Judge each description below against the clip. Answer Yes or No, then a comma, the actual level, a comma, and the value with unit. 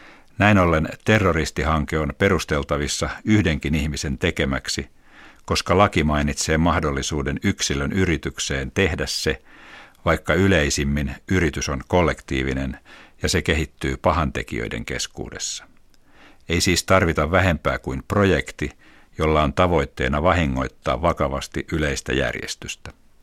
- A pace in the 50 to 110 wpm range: Yes, average, 100 wpm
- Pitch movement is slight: No, average, 4.2 semitones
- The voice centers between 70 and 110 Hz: Yes, very low, 80 Hz